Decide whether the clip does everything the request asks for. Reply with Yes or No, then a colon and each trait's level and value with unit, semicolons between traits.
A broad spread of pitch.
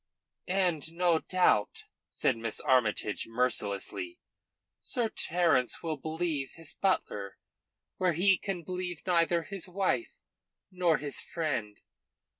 Yes: wide, 5.7 semitones